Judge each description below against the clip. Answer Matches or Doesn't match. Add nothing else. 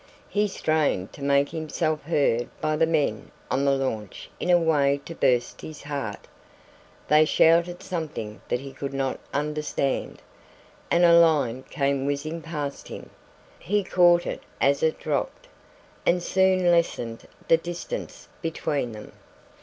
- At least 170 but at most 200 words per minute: Doesn't match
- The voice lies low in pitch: Doesn't match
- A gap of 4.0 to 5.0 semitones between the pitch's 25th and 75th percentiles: Doesn't match